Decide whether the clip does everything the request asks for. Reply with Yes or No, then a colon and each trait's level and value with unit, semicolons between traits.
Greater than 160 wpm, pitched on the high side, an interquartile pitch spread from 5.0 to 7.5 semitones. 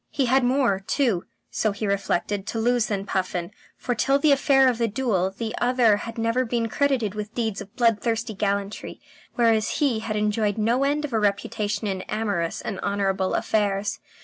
No: average, 180 wpm; high, 220 Hz; average, 3.3 semitones